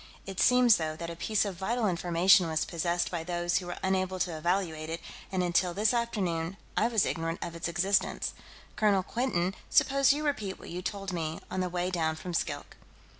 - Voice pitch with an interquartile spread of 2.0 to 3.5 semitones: Yes, average, 2.9 semitones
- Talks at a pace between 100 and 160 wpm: No, average, 200 wpm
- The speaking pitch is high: No, medium, 180 Hz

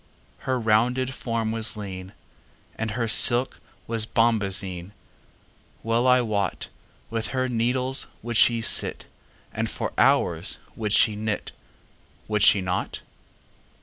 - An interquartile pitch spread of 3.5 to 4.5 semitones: No, narrow, 2.4 semitones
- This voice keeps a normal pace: No, slow, 100 wpm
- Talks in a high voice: No, low, 115 Hz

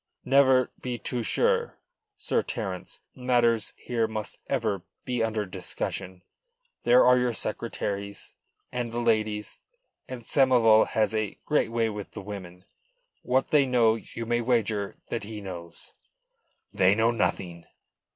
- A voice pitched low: Yes, low, 115 Hz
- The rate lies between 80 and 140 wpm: Yes, slow, 135 wpm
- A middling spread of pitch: Yes, average, 3.2 semitones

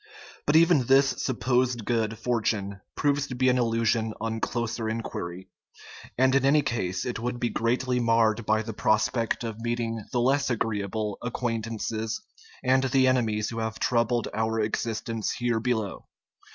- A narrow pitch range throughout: Yes, narrow, 2.2 semitones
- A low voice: Yes, low, 115 Hz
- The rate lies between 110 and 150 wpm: No, average, 160 wpm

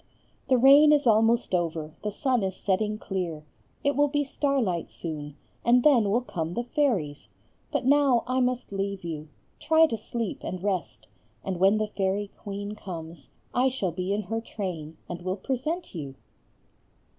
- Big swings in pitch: Yes, wide, 6.0 semitones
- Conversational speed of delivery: Yes, average, 170 wpm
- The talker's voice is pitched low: No, high, 205 Hz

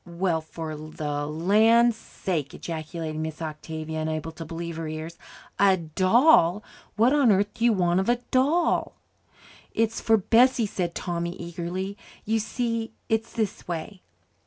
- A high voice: No, medium, 175 Hz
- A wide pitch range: Yes, wide, 5.7 semitones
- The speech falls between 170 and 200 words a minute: No, average, 145 wpm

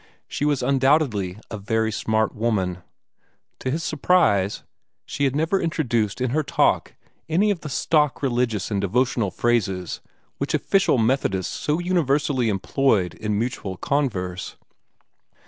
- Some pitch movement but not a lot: No, wide, 6.0 semitones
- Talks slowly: Yes, slow, 130 wpm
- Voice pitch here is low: Yes, low, 125 Hz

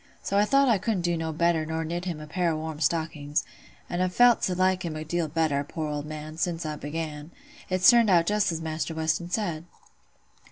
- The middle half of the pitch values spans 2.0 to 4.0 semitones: Yes, average, 2.8 semitones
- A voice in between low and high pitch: Yes, medium, 165 Hz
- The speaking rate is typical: No, fast, 215 wpm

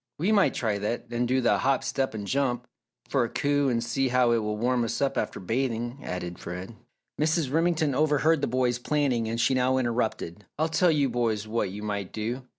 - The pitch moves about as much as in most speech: Yes, average, 3.8 semitones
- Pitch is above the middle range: No, low, 125 Hz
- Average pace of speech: No, fast, 210 wpm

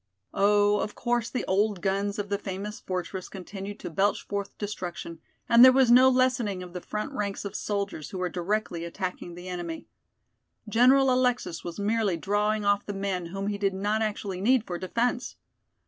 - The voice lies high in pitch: Yes, high, 200 Hz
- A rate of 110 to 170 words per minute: No, average, 180 wpm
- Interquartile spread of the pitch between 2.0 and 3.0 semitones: Yes, average, 2.7 semitones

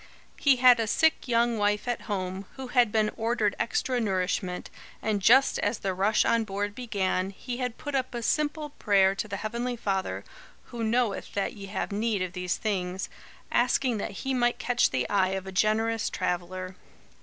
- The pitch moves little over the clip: No, average, 3.9 semitones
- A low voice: No, high, 215 Hz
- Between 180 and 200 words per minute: Yes, average, 185 wpm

